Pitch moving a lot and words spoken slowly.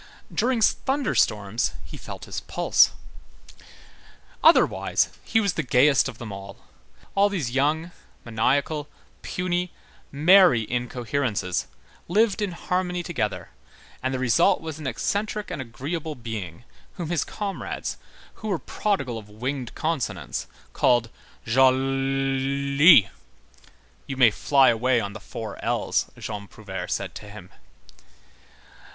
Yes: wide, 6.9 semitones; slow, 120 wpm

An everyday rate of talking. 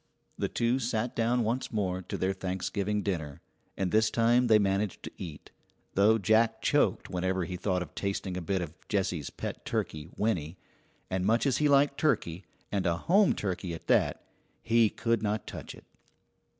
Yes: average, 175 wpm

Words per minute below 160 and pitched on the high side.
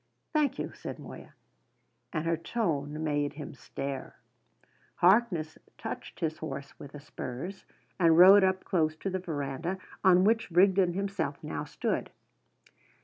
No: average, 140 wpm; medium, 165 Hz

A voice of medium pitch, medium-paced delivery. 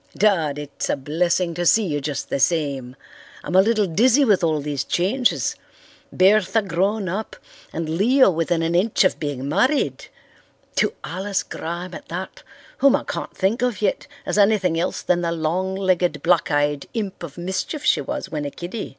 Yes: medium, 180 Hz; average, 180 wpm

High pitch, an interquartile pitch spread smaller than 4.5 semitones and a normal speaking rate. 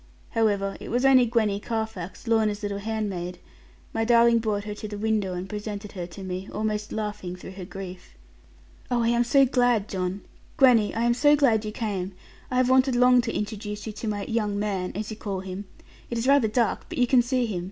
No: high, 215 Hz; average, 2.9 semitones; fast, 215 wpm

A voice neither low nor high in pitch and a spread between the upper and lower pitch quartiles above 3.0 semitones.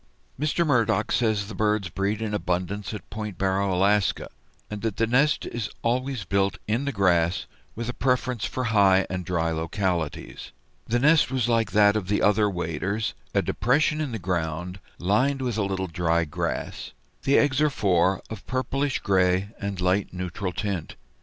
No: low, 100 Hz; average, 4.4 semitones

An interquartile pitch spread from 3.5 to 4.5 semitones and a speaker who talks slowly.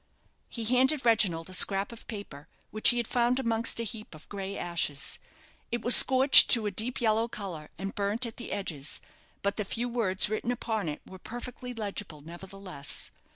No: average, 3.9 semitones; average, 185 wpm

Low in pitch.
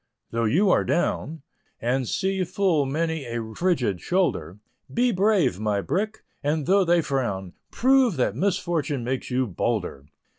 No: medium, 150 Hz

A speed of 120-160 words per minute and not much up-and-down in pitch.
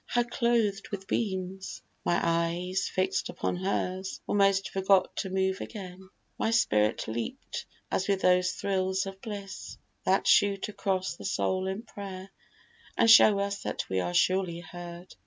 Yes: average, 155 wpm; narrow, 1.5 semitones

